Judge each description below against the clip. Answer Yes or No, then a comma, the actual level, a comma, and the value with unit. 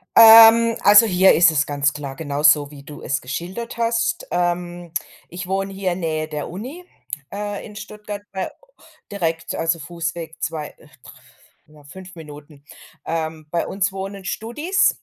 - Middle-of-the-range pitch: Yes, medium, 175 Hz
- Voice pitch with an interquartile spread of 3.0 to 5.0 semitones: Yes, average, 4.7 semitones